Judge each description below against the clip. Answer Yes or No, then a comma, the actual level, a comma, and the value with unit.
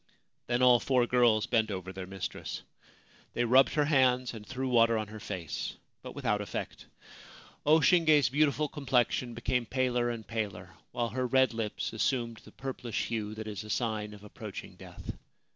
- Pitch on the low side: Yes, low, 120 Hz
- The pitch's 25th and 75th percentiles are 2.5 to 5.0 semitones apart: Yes, average, 3.1 semitones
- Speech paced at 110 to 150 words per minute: No, average, 170 wpm